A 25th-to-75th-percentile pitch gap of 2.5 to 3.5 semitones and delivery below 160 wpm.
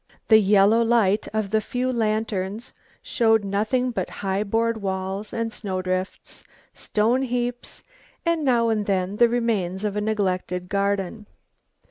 Yes: average, 2.9 semitones; average, 140 wpm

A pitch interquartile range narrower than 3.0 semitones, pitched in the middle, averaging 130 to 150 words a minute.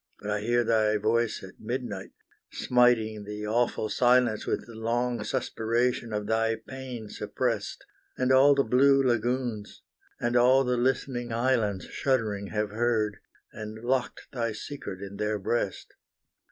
No: narrow, 2.6 semitones; low, 115 Hz; average, 140 wpm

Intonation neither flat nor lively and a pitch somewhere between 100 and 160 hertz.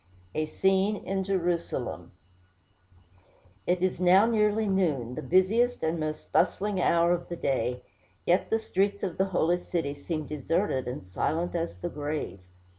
No: average, 3.8 semitones; medium, 175 Hz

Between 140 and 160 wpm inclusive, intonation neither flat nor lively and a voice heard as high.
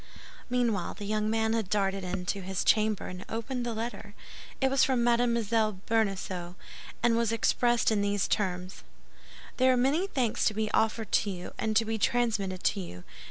No: average, 180 wpm; average, 3.2 semitones; high, 220 Hz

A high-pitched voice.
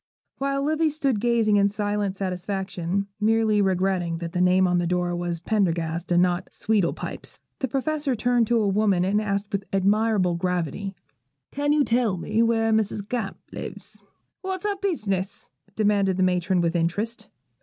Yes: high, 200 Hz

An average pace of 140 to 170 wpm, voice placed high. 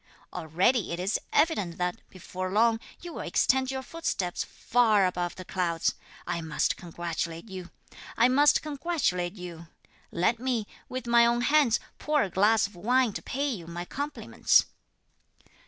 Yes: average, 155 wpm; high, 210 Hz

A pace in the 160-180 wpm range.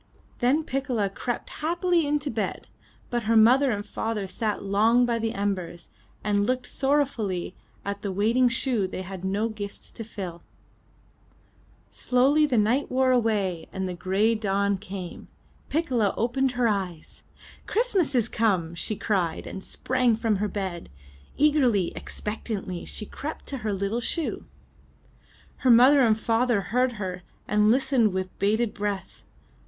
No: average, 150 wpm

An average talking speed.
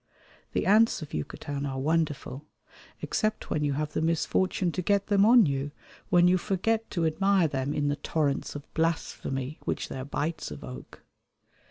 Yes: average, 165 wpm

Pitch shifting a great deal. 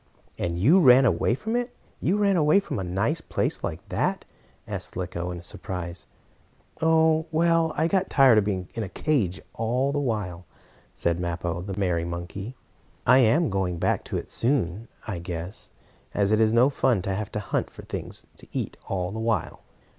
Yes: wide, 8.1 semitones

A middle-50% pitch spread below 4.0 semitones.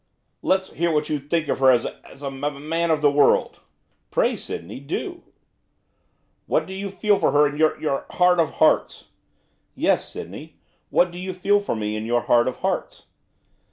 No: average, 4.6 semitones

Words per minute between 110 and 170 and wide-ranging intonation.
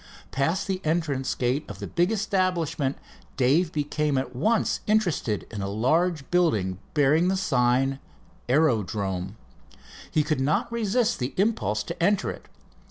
Yes: average, 140 wpm; wide, 6.4 semitones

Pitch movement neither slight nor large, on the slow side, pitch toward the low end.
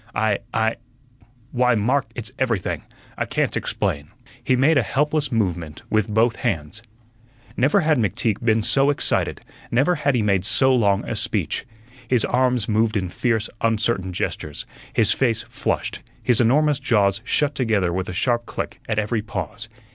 No: average, 3.8 semitones; average, 160 wpm; low, 115 Hz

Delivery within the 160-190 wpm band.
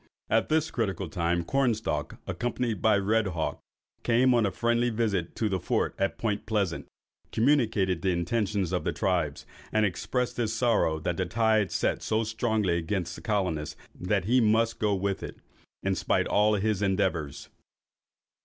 Yes: average, 165 wpm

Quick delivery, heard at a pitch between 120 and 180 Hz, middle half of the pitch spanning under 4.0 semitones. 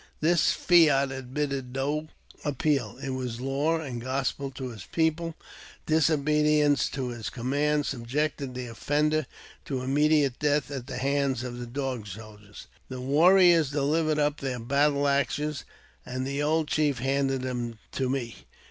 No: average, 145 wpm; medium, 140 Hz; average, 2.9 semitones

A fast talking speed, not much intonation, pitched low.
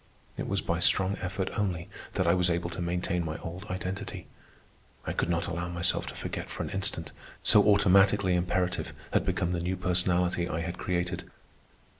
No: average, 180 wpm; narrow, 1.5 semitones; very low, 90 Hz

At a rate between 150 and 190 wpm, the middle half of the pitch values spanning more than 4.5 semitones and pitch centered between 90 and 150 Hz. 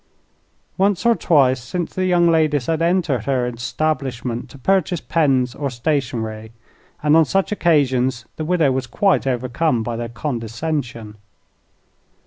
No: slow, 135 wpm; average, 5.1 semitones; low, 135 Hz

